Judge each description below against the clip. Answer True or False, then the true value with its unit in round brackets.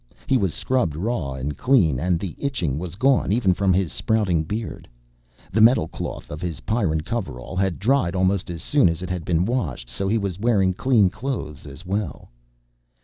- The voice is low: True (95 Hz)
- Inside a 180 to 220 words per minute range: True (185 wpm)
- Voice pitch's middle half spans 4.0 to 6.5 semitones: True (5.3 semitones)